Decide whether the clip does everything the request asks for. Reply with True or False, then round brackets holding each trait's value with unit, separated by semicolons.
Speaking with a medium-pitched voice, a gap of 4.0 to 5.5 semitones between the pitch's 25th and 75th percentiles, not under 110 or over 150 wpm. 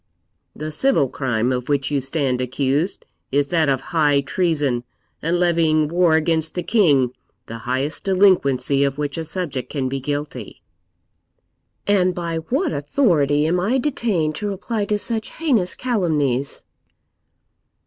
True (155 Hz; 4.8 semitones; 140 wpm)